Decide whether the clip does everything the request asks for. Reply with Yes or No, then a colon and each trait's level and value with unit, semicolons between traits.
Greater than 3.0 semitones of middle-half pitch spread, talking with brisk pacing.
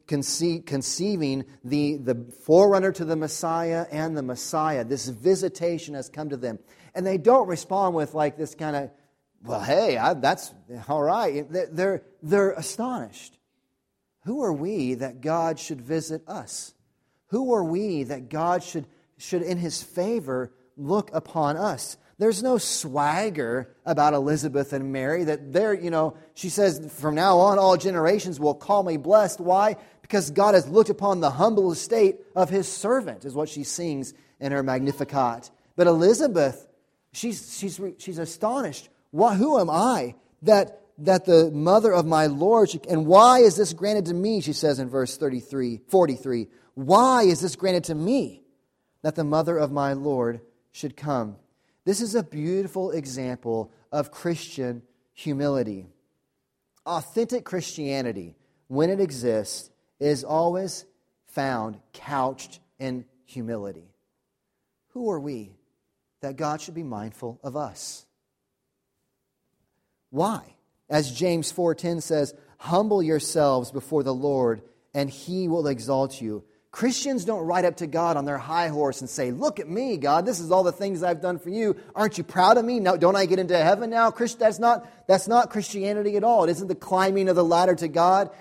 No: wide, 5.4 semitones; average, 160 wpm